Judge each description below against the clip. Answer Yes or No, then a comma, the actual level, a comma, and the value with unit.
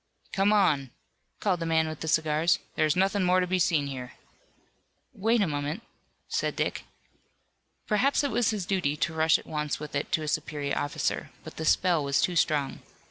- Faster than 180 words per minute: Yes, average, 190 wpm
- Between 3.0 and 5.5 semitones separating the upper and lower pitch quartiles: Yes, average, 4.1 semitones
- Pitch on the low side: No, medium, 160 Hz